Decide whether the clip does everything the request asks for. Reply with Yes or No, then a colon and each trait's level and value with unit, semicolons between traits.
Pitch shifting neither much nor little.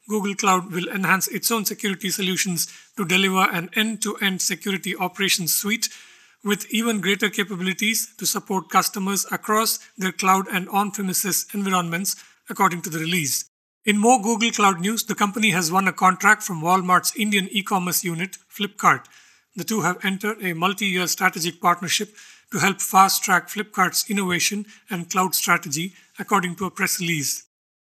No: narrow, 2.2 semitones